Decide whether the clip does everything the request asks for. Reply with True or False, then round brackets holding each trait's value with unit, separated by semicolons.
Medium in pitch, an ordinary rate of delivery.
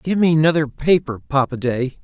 True (145 Hz; 175 wpm)